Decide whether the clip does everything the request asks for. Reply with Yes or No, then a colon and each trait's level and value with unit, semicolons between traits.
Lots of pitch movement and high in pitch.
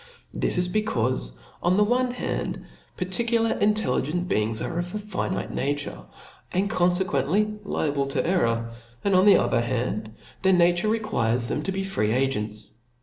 No: wide, 8.0 semitones; medium, 180 Hz